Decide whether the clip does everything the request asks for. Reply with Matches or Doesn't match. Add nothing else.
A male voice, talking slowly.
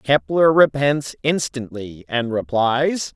Matches